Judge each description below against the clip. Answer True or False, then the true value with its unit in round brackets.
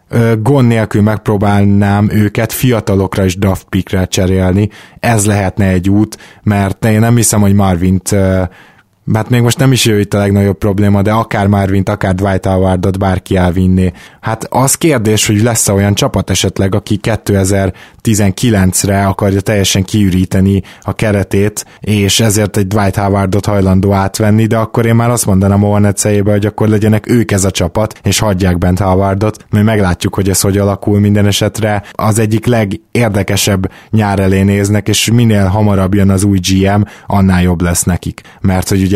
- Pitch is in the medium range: False (100 Hz)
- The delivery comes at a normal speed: False (165 wpm)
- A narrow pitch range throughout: True (1.9 semitones)